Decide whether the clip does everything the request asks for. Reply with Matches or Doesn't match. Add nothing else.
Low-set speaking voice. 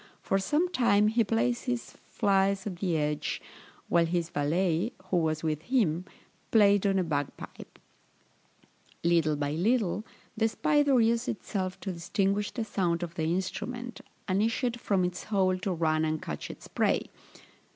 Doesn't match